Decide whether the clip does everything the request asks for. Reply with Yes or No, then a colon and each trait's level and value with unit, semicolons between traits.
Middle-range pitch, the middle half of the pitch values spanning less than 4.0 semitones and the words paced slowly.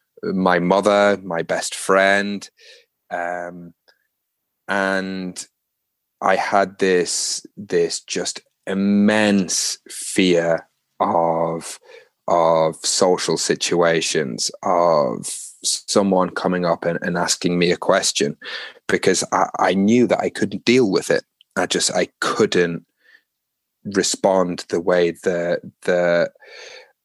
No: very low, 90 Hz; narrow, 2.4 semitones; slow, 105 wpm